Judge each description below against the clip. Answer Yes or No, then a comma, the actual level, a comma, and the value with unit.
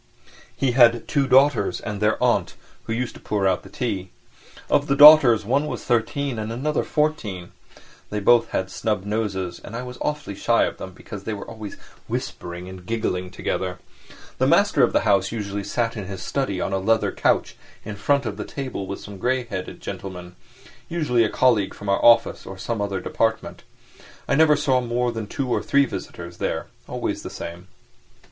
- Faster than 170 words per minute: Yes, average, 190 wpm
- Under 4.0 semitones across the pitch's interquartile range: No, average, 4.5 semitones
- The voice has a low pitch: Yes, low, 110 Hz